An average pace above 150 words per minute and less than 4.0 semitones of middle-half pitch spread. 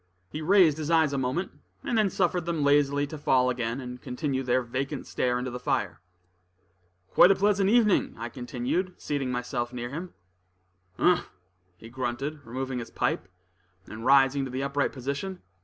No: average, 170 wpm; average, 4.4 semitones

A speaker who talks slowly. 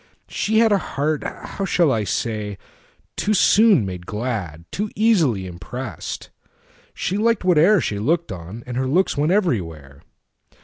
Yes: slow, 120 wpm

